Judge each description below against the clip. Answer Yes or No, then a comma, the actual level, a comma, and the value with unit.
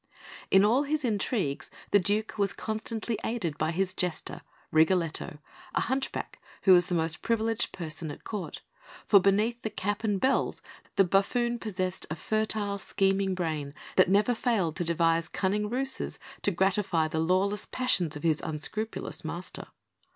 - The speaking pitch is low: No, high, 195 Hz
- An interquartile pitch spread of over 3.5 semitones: Yes, average, 4.4 semitones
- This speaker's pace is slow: No, average, 155 wpm